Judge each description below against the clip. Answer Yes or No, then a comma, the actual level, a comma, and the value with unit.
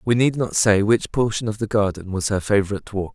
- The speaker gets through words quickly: Yes, fast, 250 wpm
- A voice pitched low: Yes, low, 105 Hz